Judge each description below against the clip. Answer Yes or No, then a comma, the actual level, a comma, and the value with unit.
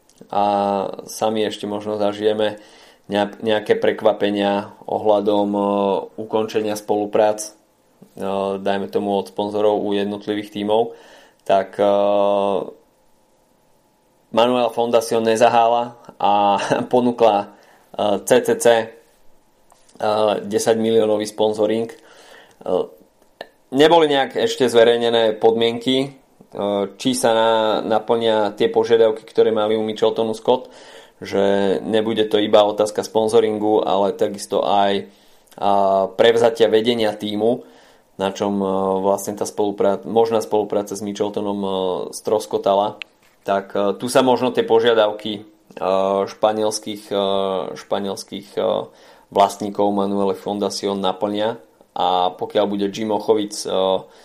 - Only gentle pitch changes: Yes, narrow, 1.8 semitones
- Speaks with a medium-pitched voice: No, low, 105 Hz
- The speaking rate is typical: No, slow, 90 wpm